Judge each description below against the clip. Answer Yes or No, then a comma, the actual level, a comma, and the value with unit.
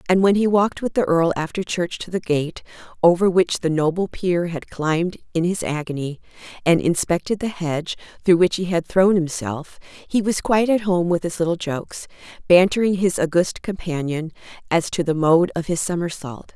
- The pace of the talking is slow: No, average, 190 wpm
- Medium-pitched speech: Yes, medium, 175 Hz